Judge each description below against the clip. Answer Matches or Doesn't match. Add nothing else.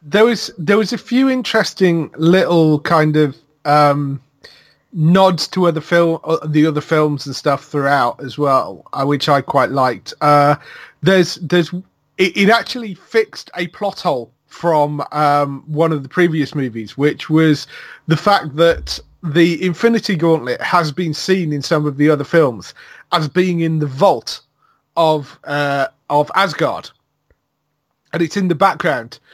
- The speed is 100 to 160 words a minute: Matches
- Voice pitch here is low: Doesn't match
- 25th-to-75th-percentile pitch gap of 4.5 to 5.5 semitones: Doesn't match